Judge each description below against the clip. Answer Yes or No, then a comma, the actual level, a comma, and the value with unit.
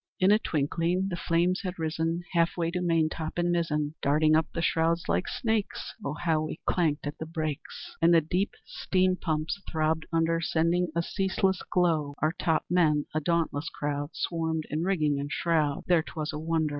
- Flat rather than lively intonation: Yes, narrow, 2.1 semitones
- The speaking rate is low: No, average, 185 wpm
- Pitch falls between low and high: Yes, medium, 165 Hz